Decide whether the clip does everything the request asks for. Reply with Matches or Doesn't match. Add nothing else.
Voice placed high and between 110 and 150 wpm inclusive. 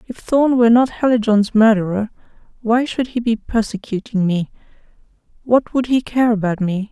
Matches